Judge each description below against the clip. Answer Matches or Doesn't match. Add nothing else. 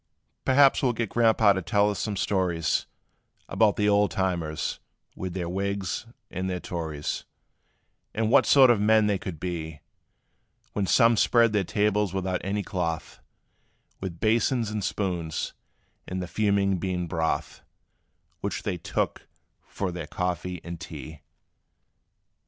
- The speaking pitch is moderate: Doesn't match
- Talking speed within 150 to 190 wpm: Doesn't match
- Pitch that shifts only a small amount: Doesn't match